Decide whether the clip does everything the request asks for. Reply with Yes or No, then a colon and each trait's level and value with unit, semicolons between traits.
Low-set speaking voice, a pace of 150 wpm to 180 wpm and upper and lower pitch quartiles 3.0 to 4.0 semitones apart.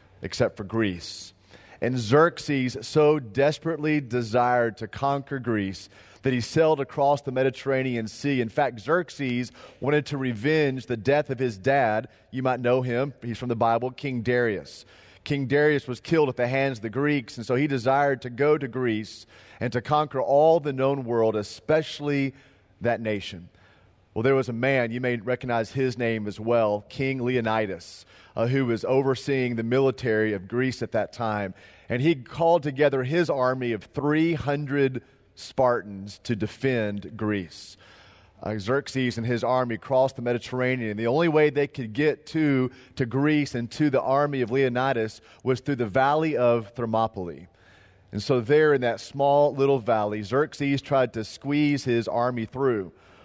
Yes: low, 125 Hz; average, 165 wpm; average, 3.7 semitones